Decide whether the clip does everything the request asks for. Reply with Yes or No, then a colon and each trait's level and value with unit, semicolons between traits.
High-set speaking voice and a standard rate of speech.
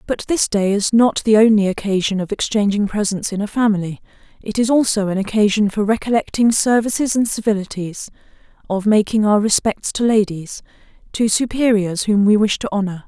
Yes: high, 210 Hz; average, 170 wpm